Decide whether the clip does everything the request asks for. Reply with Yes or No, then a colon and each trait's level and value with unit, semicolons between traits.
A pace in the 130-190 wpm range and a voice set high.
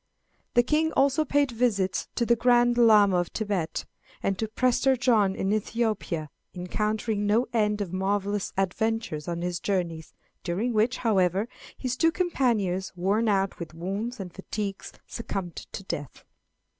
Yes: average, 145 wpm; high, 210 Hz